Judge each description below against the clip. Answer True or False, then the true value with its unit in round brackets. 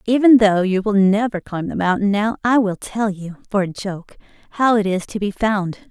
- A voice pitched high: True (205 Hz)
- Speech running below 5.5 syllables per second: True (4.9 syllables/s)